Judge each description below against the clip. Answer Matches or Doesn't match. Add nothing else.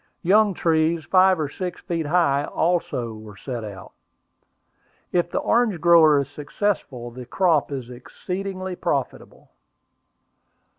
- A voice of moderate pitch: Matches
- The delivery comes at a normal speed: Doesn't match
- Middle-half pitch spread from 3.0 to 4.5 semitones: Doesn't match